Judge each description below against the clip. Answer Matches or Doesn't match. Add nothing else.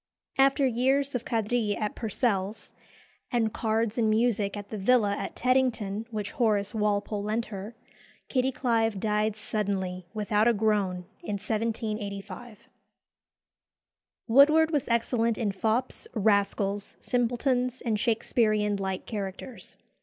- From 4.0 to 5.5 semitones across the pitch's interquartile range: Doesn't match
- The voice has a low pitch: Doesn't match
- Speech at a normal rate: Doesn't match